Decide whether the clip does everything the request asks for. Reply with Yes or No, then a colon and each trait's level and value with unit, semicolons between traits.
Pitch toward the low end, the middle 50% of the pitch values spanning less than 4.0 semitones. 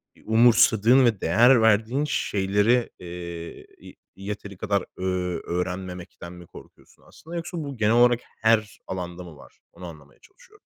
No: low, 100 Hz; average, 4.6 semitones